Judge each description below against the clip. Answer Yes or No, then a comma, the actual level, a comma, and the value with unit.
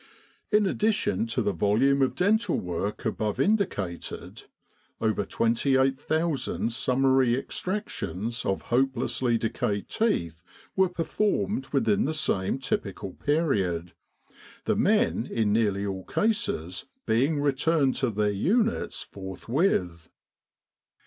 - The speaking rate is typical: No, slow, 110 wpm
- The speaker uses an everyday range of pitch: No, wide, 7.8 semitones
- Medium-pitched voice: No, low, 125 Hz